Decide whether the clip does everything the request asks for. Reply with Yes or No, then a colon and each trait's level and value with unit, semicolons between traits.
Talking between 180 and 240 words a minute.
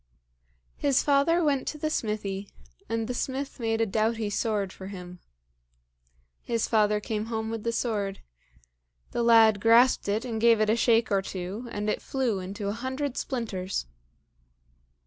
No: average, 160 wpm